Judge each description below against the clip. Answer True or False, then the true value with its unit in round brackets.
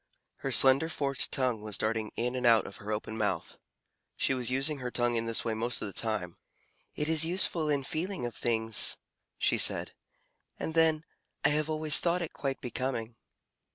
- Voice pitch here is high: False (130 Hz)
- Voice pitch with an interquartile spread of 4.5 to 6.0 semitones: True (5.1 semitones)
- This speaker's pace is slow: False (190 wpm)